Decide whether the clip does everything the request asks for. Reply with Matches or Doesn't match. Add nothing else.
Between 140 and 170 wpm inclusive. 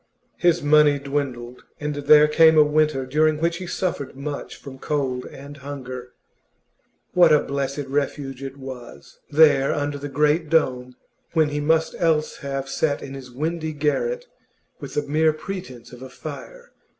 Matches